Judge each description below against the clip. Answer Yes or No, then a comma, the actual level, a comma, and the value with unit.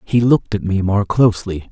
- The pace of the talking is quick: Yes, fast, 210 wpm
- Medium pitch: No, low, 105 Hz